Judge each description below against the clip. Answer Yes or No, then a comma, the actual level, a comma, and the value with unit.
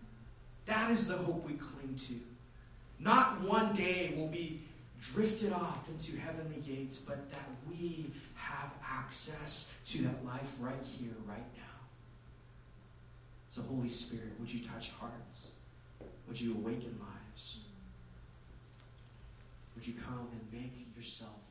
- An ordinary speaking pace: No, slow, 130 wpm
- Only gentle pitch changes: No, average, 4.1 semitones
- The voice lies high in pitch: No, low, 120 Hz